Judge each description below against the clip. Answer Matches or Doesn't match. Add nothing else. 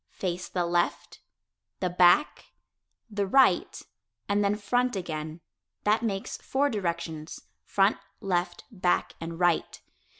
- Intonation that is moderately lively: Matches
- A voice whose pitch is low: Doesn't match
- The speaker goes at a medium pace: Doesn't match